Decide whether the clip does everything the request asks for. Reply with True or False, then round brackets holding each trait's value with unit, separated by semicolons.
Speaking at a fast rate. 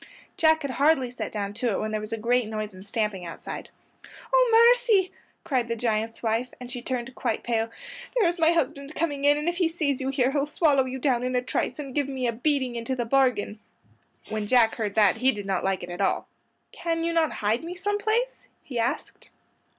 True (220 wpm)